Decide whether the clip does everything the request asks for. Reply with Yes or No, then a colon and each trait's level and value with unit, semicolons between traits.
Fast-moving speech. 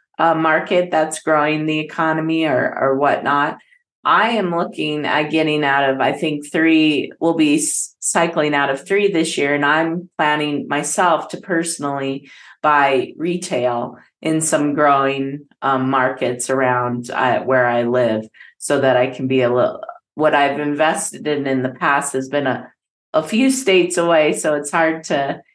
No: average, 165 wpm